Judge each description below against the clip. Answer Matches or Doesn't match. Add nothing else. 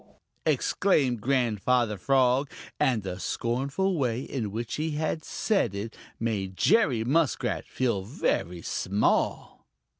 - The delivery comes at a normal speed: Doesn't match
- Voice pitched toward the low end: Matches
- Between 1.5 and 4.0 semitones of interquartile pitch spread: Doesn't match